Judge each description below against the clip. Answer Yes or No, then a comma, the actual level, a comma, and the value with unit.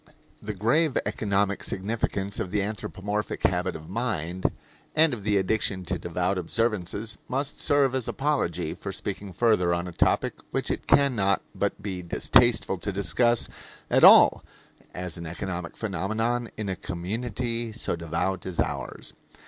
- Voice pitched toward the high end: No, low, 100 Hz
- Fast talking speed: No, average, 150 wpm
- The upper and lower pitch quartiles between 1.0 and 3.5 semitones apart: No, average, 4.2 semitones